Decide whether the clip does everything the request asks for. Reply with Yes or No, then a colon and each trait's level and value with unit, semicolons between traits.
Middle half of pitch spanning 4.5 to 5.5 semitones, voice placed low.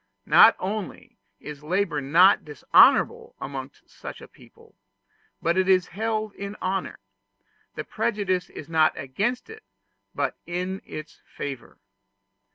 No: average, 4.9 semitones; medium, 185 Hz